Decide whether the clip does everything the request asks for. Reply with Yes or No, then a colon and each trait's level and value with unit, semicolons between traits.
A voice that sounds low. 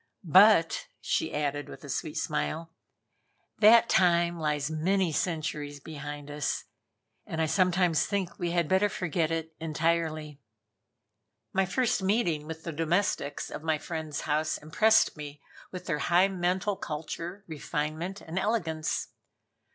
No: medium, 165 Hz